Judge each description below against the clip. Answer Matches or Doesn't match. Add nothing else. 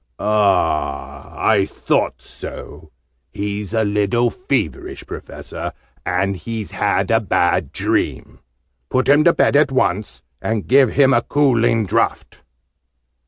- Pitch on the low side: Matches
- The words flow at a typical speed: Doesn't match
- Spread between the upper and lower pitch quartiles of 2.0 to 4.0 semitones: Doesn't match